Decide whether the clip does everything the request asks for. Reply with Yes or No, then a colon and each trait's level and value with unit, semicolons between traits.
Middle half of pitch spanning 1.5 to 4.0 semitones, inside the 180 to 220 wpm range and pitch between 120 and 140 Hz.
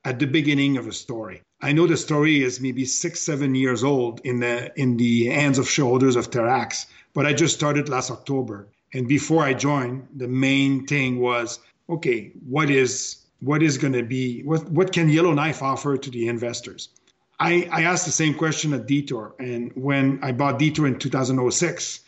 Yes: average, 3.0 semitones; average, 200 wpm; low, 135 Hz